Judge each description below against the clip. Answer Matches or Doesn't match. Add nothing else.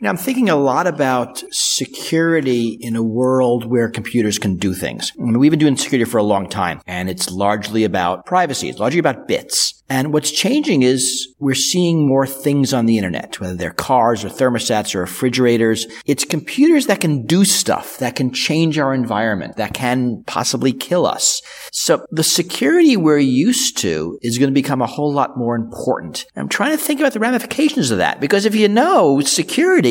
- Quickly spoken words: Doesn't match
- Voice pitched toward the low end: Matches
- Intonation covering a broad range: Matches